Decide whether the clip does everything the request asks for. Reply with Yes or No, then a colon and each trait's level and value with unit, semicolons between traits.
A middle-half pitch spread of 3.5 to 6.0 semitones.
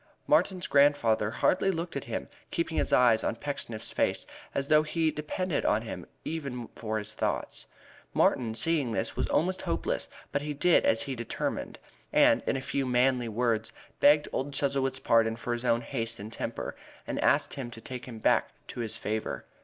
Yes: average, 4.2 semitones